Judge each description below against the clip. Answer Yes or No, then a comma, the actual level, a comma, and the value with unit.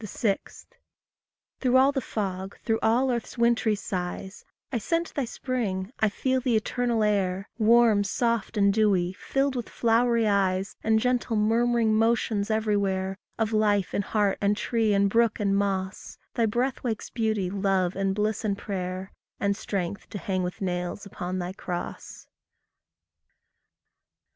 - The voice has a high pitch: Yes, high, 210 Hz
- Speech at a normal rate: Yes, average, 150 wpm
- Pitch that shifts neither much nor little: Yes, average, 3.1 semitones